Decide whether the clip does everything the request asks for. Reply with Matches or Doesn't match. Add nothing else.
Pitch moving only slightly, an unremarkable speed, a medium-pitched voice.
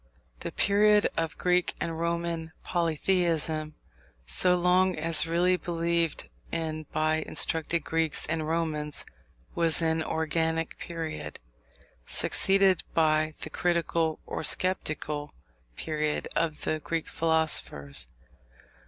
Doesn't match